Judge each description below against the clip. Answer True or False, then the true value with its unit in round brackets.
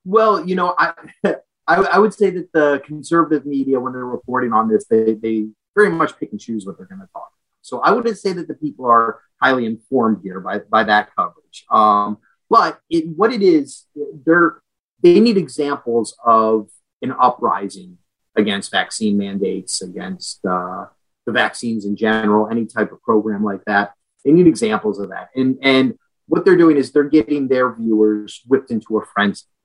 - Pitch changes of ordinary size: False (6.9 semitones)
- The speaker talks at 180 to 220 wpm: True (185 wpm)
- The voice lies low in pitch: True (125 Hz)